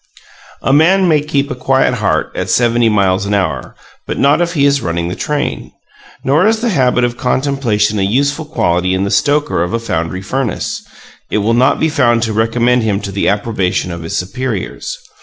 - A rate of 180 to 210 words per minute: Yes, average, 195 wpm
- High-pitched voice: No, low, 120 Hz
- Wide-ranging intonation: Yes, wide, 6.1 semitones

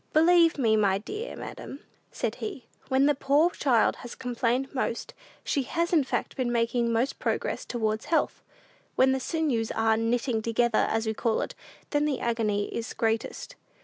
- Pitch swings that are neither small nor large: Yes, average, 4.0 semitones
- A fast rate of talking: No, average, 170 wpm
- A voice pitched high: Yes, high, 245 Hz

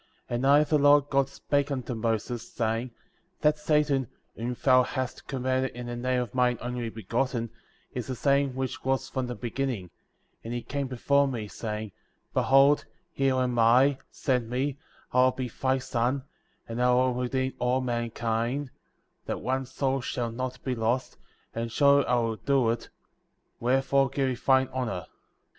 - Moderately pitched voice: No, low, 130 Hz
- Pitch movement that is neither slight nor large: No, narrow, 2.1 semitones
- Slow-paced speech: No, average, 170 wpm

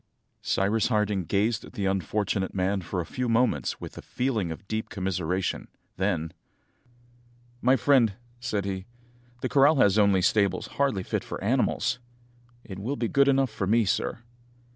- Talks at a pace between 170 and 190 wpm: No, average, 160 wpm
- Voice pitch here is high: No, low, 105 Hz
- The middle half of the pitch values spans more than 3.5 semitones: Yes, average, 3.9 semitones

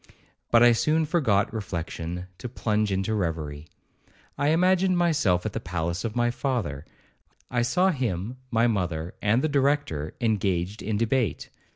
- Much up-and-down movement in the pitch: Yes, wide, 6.8 semitones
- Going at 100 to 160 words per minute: Yes, average, 150 wpm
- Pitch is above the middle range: No, low, 110 Hz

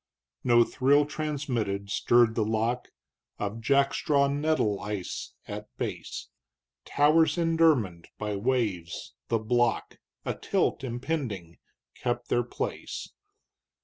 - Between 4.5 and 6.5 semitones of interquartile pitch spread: Yes, average, 5.0 semitones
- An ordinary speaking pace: No, slow, 105 wpm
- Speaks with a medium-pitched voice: No, low, 120 Hz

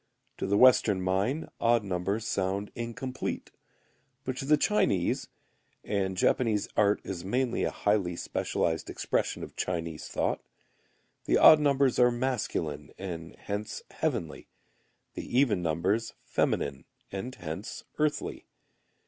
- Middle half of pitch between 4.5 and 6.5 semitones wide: Yes, average, 5.3 semitones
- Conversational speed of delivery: No, slow, 125 wpm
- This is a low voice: Yes, low, 105 Hz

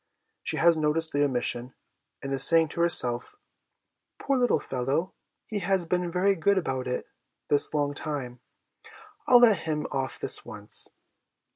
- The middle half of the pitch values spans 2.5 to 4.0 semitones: No, average, 5.0 semitones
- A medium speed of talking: Yes, average, 155 wpm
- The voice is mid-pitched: Yes, medium, 155 Hz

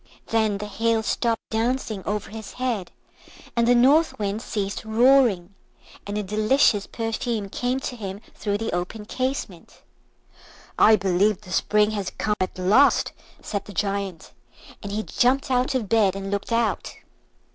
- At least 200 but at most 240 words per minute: No, average, 155 wpm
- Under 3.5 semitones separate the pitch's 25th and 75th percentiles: Yes, average, 2.8 semitones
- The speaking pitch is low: No, high, 215 Hz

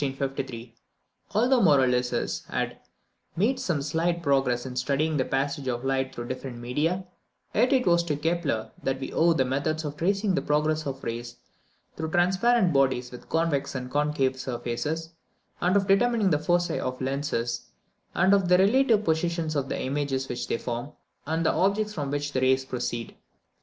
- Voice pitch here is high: No, medium, 150 Hz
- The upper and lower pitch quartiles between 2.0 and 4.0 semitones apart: No, average, 4.9 semitones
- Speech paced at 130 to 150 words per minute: No, average, 170 wpm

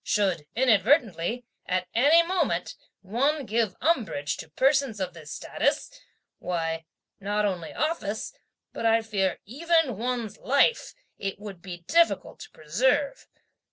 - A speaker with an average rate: No, slow, 125 wpm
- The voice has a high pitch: Yes, high, 220 Hz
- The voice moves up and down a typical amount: No, wide, 6.9 semitones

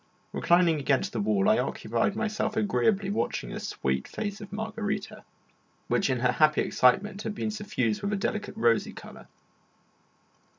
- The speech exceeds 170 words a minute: No, average, 155 wpm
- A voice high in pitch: Yes, high, 195 Hz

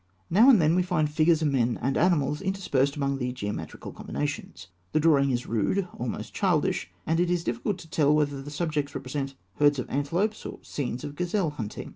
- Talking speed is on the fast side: No, average, 195 wpm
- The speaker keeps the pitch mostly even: No, average, 3.9 semitones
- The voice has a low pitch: No, medium, 145 Hz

